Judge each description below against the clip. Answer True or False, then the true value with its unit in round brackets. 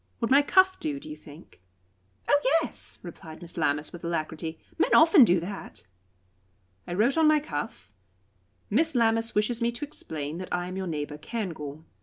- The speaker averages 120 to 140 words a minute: False (175 wpm)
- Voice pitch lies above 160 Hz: True (190 Hz)